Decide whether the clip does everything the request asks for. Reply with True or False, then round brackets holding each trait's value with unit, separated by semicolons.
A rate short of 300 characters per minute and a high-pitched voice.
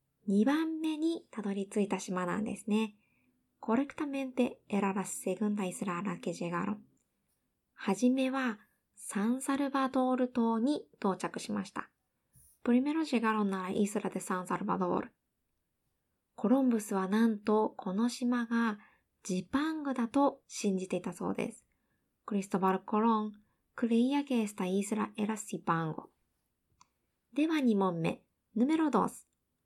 False (305 characters per minute; 215 Hz)